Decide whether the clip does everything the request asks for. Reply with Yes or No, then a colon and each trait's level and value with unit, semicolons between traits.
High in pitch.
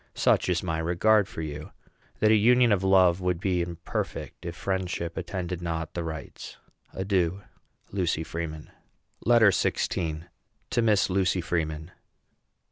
No: very low, 90 Hz